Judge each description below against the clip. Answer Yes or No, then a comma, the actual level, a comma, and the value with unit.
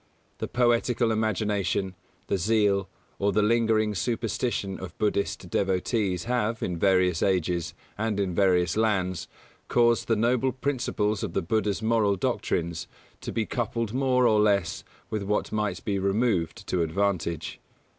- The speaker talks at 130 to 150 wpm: Yes, average, 140 wpm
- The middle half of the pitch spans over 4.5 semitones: No, average, 3.2 semitones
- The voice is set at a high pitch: No, low, 105 Hz